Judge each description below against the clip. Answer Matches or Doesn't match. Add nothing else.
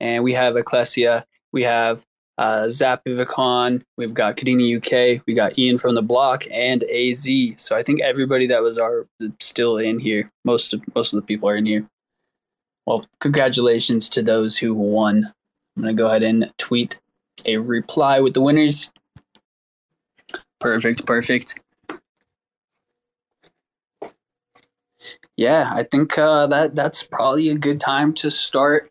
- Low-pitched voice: Matches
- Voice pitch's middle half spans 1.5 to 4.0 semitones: Matches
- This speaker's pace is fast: Doesn't match